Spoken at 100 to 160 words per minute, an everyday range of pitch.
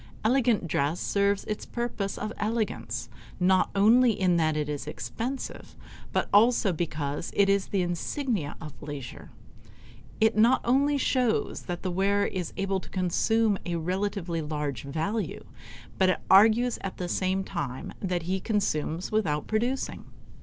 Yes: average, 145 wpm; average, 5.0 semitones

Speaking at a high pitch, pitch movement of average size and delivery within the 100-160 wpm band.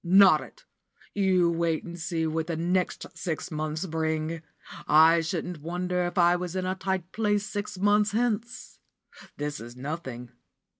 No: medium, 175 Hz; average, 3.0 semitones; average, 155 wpm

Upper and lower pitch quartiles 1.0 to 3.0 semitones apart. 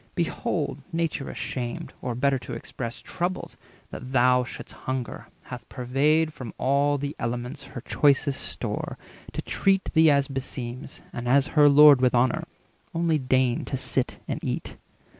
Yes: average, 2.7 semitones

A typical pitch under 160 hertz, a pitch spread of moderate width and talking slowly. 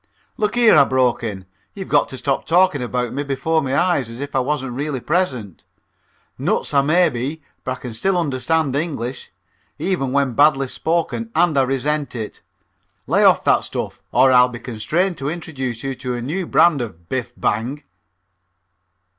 No: low, 135 Hz; average, 4.3 semitones; average, 175 wpm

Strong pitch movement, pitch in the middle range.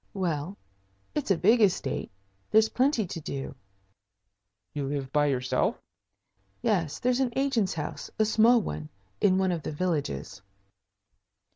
Yes: wide, 7.3 semitones; medium, 180 Hz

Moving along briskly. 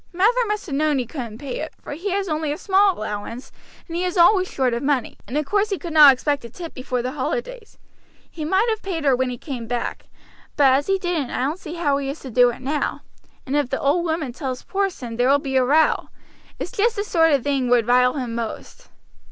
Yes: fast, 245 wpm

